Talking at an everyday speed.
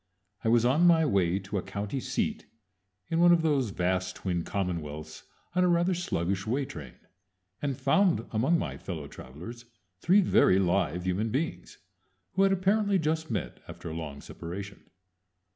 Yes: average, 160 wpm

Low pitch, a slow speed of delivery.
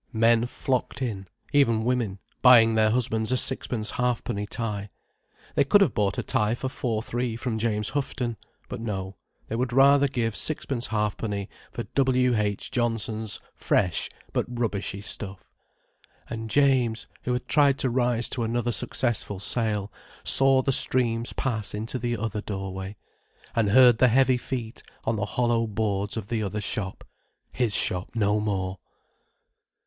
No: low, 115 Hz; average, 150 wpm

